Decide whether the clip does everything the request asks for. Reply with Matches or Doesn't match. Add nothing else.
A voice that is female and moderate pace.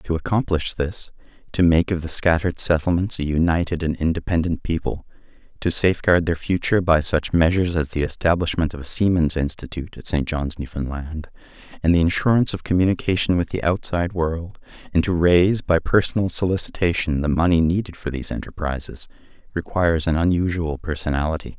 Doesn't match